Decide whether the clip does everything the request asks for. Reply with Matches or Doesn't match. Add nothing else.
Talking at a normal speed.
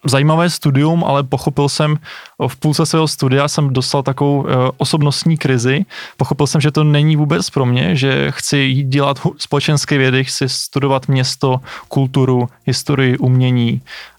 Matches